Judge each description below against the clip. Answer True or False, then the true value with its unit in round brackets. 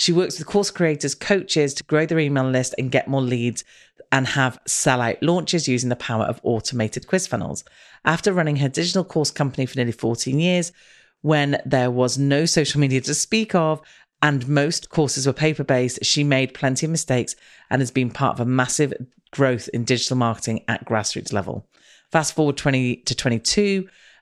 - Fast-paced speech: False (190 wpm)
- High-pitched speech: False (140 Hz)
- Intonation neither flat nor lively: True (3.8 semitones)